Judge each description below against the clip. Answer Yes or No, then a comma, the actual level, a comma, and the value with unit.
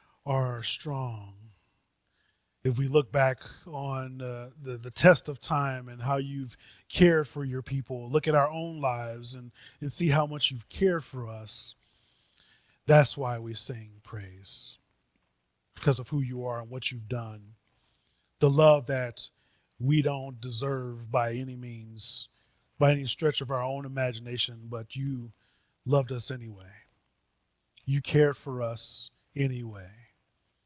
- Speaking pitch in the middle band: No, low, 130 Hz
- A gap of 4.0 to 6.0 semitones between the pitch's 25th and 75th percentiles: No, average, 3.0 semitones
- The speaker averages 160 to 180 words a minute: No, average, 145 wpm